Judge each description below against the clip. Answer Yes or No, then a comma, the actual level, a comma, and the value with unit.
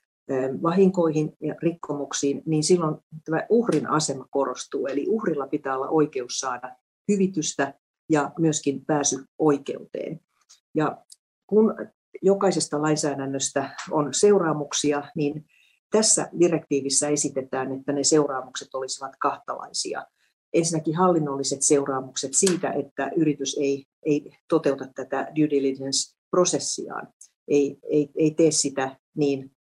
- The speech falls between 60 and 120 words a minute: Yes, average, 105 wpm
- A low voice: No, medium, 145 Hz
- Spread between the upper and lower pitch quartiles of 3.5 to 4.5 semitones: No, narrow, 2.6 semitones